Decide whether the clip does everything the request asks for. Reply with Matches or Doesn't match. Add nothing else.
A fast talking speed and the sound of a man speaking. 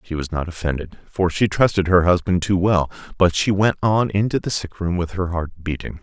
Matches